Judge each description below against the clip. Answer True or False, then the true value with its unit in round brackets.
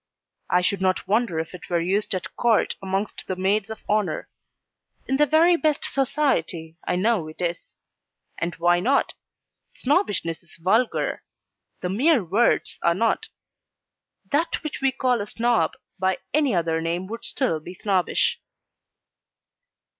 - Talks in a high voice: True (200 Hz)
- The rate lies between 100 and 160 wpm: True (145 wpm)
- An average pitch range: False (6.5 semitones)